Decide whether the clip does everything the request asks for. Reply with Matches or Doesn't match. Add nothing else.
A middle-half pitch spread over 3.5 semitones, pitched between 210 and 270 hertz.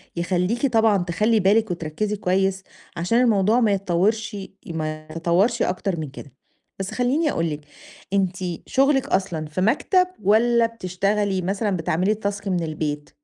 Doesn't match